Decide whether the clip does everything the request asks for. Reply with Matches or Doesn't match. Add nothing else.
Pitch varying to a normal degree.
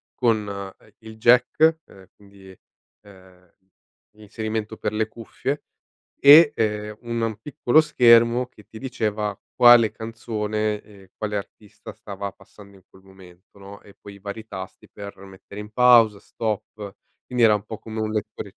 Doesn't match